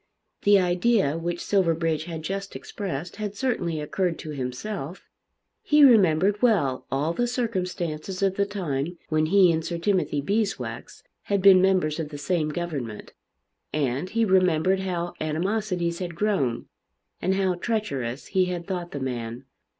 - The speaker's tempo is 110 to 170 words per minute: Yes, average, 150 wpm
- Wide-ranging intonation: No, average, 4.2 semitones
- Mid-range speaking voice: Yes, medium, 175 Hz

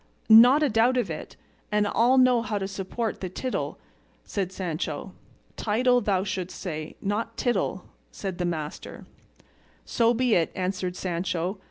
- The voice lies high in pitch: Yes, high, 200 Hz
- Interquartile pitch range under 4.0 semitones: No, average, 4.3 semitones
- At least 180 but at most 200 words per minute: No, average, 150 wpm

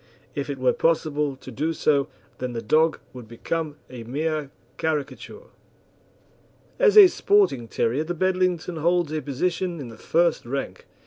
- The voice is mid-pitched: Yes, medium, 155 Hz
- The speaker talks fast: No, average, 150 wpm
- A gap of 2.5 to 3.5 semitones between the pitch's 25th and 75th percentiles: No, average, 4.4 semitones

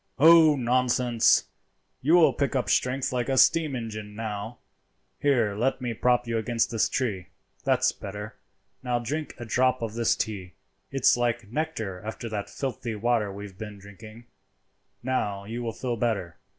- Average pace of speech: Yes, average, 165 wpm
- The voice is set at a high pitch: No, low, 120 Hz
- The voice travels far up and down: No, average, 3.2 semitones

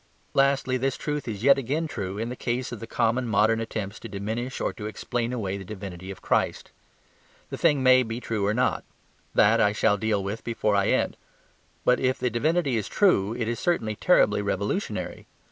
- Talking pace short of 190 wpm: No, average, 195 wpm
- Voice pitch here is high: No, low, 115 Hz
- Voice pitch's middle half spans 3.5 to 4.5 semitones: Yes, average, 3.8 semitones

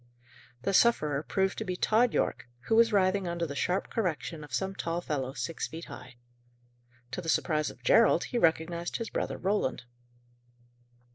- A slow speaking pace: No, average, 165 wpm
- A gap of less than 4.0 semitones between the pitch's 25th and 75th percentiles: No, average, 4.5 semitones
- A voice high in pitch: No, medium, 175 Hz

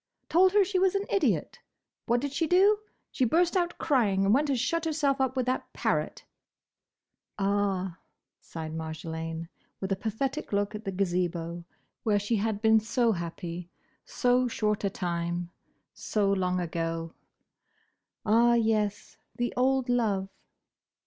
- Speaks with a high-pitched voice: Yes, high, 215 Hz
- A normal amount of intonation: No, wide, 6.4 semitones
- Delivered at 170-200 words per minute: No, average, 145 wpm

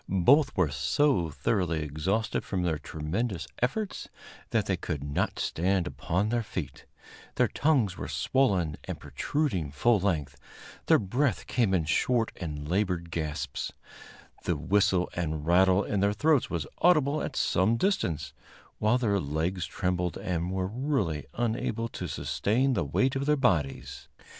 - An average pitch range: No, wide, 6.8 semitones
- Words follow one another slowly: No, average, 150 wpm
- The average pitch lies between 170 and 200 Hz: No, very low, 95 Hz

